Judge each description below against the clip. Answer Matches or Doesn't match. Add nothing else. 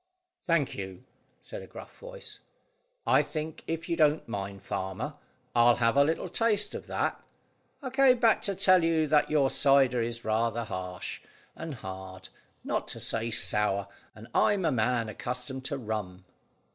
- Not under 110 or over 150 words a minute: Doesn't match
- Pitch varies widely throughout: Matches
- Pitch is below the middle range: Matches